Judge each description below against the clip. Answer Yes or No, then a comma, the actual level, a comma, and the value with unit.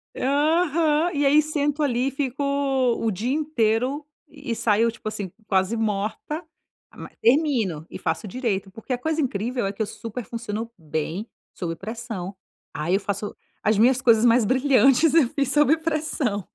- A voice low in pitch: No, high, 240 Hz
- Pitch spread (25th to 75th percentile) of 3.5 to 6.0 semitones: Yes, wide, 5.4 semitones